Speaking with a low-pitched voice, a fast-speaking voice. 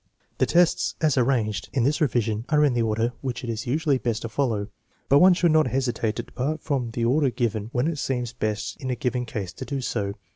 Yes: low, 125 Hz; fast, 240 wpm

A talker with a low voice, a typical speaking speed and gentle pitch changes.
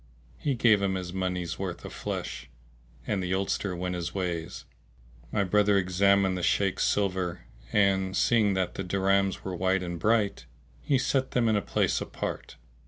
Yes: very low, 95 Hz; average, 170 wpm; narrow, 1.9 semitones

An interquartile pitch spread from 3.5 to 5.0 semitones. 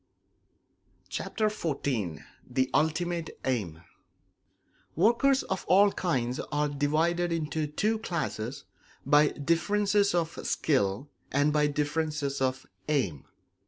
Yes: average, 4.3 semitones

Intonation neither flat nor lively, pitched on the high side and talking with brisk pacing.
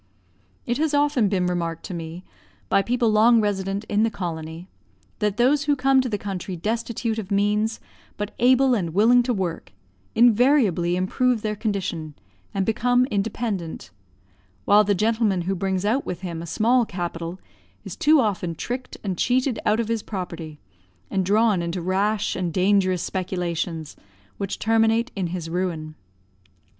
No: average, 4.4 semitones; high, 205 Hz; average, 155 wpm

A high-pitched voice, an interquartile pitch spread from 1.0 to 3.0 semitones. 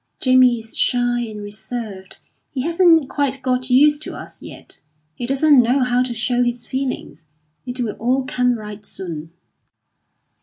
Yes: high, 245 Hz; narrow, 2.6 semitones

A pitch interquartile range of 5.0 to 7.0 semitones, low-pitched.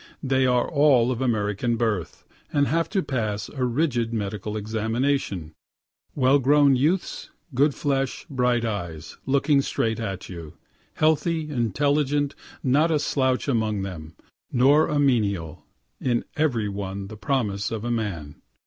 Yes: average, 5.3 semitones; low, 120 Hz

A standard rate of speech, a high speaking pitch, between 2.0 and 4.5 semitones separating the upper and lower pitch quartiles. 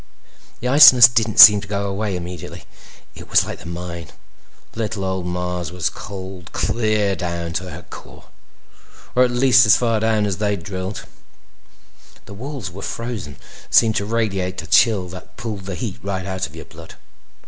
No: average, 170 wpm; low, 100 Hz; average, 3.6 semitones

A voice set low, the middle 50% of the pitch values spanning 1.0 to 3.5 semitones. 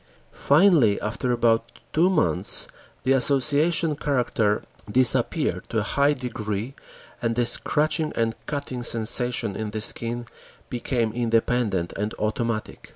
No: low, 120 Hz; average, 4.1 semitones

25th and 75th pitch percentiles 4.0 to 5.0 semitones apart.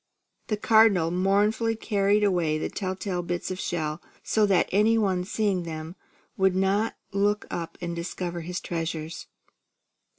No: average, 3.2 semitones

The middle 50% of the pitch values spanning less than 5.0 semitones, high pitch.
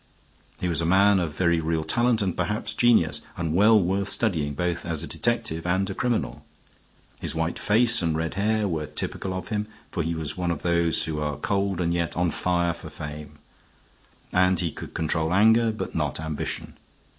No: average, 3.8 semitones; very low, 90 Hz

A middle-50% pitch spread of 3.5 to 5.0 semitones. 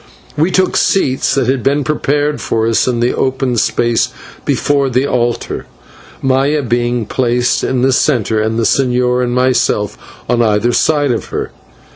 No: narrow, 2.5 semitones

